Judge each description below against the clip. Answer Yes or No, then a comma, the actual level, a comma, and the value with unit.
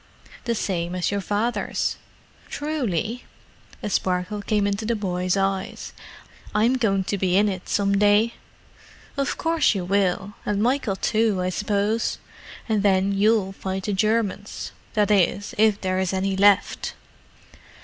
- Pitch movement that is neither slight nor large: No, narrow, 2.2 semitones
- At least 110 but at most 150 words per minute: Yes, average, 140 wpm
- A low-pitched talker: No, high, 200 Hz